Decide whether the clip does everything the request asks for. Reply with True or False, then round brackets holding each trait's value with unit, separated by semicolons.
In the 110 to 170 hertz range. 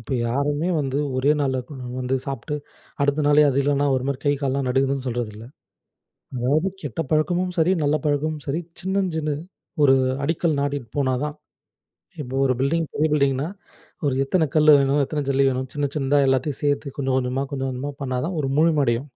True (140 Hz)